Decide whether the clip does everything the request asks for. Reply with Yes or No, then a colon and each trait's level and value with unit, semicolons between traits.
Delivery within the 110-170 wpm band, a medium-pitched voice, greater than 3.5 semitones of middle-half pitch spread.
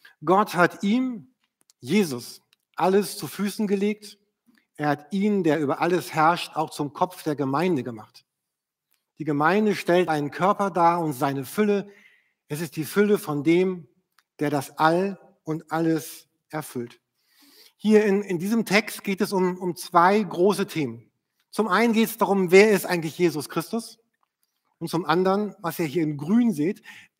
Yes: average, 160 wpm; medium, 180 Hz; average, 4.6 semitones